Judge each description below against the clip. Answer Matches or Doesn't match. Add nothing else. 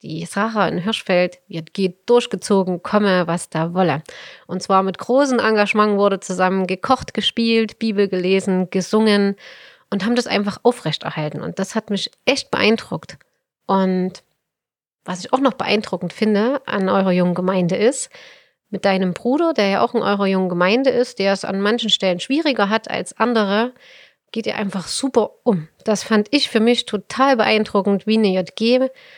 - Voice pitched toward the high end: Matches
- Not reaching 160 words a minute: Doesn't match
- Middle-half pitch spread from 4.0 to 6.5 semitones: Doesn't match